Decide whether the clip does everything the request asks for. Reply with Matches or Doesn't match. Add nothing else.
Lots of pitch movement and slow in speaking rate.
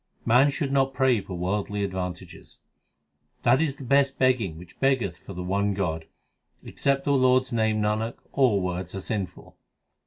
Doesn't match